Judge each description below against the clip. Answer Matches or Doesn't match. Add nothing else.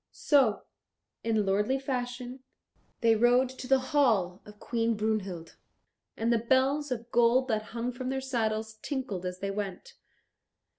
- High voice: Matches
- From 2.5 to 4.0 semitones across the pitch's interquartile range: Matches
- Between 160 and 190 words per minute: Doesn't match